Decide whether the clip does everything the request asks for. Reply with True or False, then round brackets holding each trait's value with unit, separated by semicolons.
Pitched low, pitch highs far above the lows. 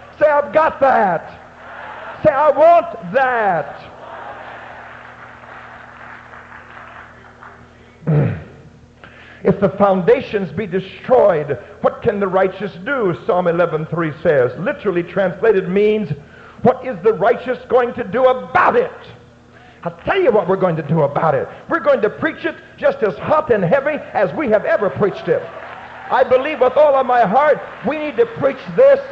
False (245 Hz; 6.9 semitones)